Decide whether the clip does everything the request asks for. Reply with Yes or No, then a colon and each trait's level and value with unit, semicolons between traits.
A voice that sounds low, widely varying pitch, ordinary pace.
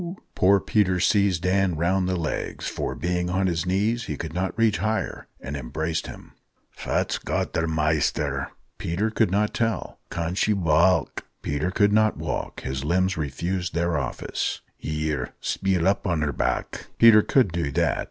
No: very low, 90 Hz; average, 3.8 semitones; average, 160 wpm